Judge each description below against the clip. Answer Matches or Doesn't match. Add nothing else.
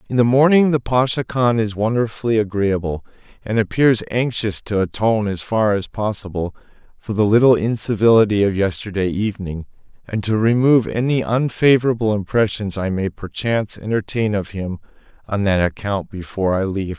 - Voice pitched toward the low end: Matches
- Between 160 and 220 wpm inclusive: Doesn't match